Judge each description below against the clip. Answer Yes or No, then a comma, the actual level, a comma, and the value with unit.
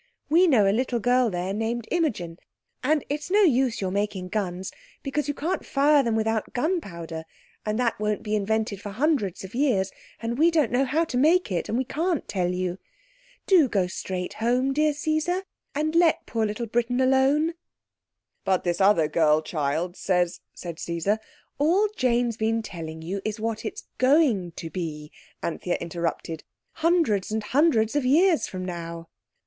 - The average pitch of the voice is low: No, high, 225 Hz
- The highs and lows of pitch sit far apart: Yes, wide, 7.8 semitones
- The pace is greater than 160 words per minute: Yes, average, 170 wpm